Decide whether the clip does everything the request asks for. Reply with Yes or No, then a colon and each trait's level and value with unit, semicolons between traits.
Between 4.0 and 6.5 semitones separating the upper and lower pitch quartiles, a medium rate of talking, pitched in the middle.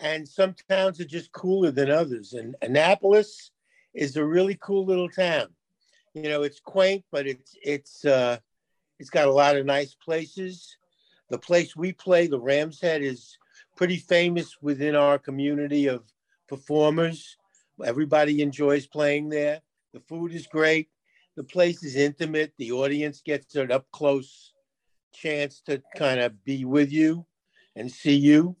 No: average, 3.5 semitones; average, 155 wpm; medium, 150 Hz